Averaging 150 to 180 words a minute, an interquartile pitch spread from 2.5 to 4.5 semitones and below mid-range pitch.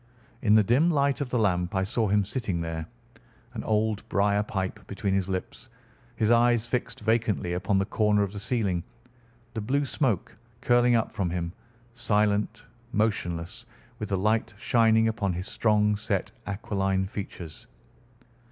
Yes: average, 155 wpm; average, 2.8 semitones; low, 105 Hz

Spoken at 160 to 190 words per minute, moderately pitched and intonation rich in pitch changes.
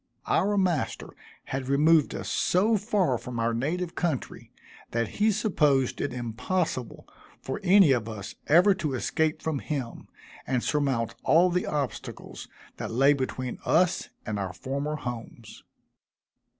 No: slow, 135 wpm; medium, 145 Hz; wide, 6.4 semitones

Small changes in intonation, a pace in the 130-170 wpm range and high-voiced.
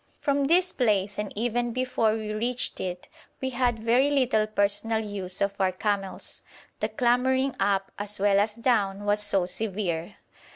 No: average, 3.5 semitones; average, 160 wpm; high, 215 Hz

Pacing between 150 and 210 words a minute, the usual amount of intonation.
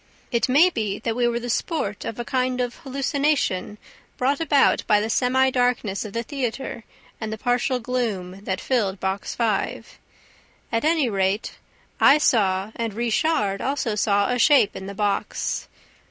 Yes: average, 165 wpm; average, 4.1 semitones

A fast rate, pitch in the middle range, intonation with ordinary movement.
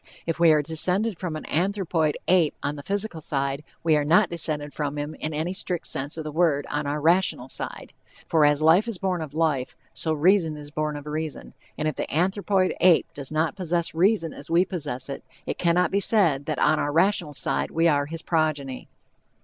Yes: fast, 210 wpm; medium, 160 Hz; average, 3.2 semitones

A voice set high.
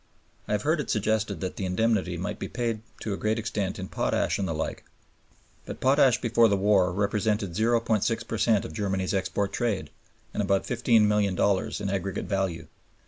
No: low, 105 Hz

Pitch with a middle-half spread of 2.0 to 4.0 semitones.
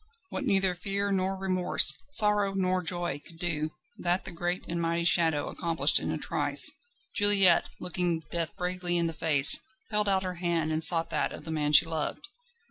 Yes: narrow, 2.4 semitones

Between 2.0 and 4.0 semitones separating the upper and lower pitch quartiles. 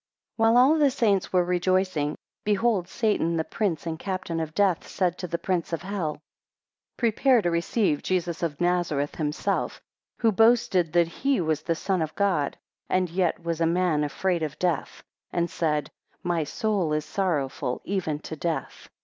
Yes: average, 3.4 semitones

